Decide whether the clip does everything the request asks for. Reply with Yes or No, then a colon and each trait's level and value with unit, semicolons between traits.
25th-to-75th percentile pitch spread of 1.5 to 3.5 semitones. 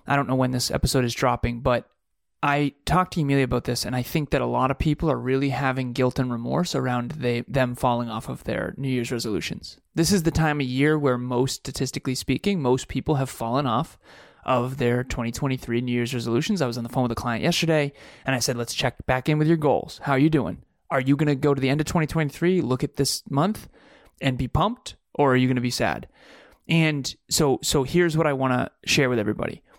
Yes: average, 3.1 semitones